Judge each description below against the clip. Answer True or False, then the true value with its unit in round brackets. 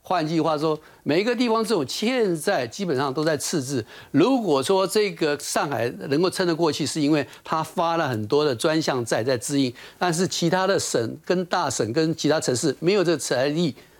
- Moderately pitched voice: True (160 Hz)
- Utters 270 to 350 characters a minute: True (290 characters per minute)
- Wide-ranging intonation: False (4.0 semitones)